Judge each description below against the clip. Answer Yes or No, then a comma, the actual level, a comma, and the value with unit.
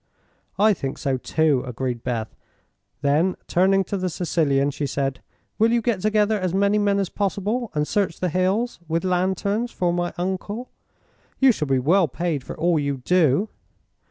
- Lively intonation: Yes, wide, 5.8 semitones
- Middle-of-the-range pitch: Yes, medium, 180 Hz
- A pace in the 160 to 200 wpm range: Yes, average, 170 wpm